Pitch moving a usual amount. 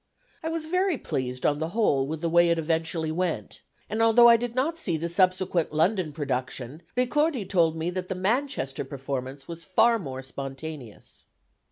No: wide, 8.0 semitones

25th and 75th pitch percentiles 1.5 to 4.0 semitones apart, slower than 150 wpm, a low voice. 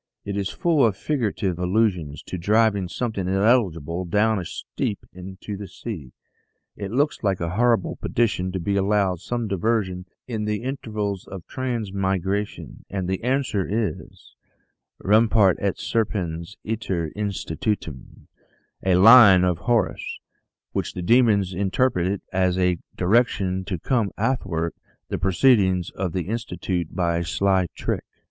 Yes: average, 3.5 semitones; average, 140 wpm; low, 100 Hz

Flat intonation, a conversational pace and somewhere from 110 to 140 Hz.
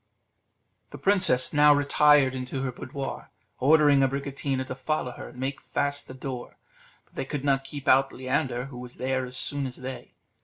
Yes: narrow, 1.8 semitones; average, 180 wpm; low, 135 Hz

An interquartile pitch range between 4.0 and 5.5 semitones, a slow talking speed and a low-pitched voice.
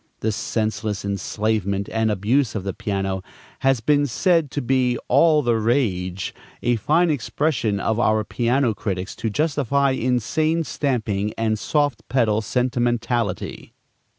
Yes: average, 4.6 semitones; slow, 130 wpm; low, 115 Hz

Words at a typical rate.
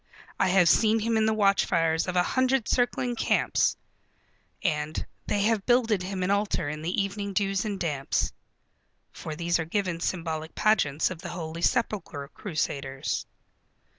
Yes: average, 155 wpm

